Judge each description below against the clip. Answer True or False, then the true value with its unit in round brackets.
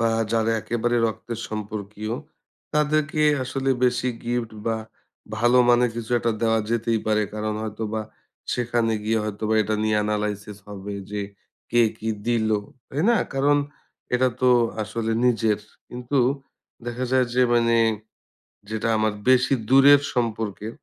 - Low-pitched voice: True (115 Hz)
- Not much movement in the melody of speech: True (2.3 semitones)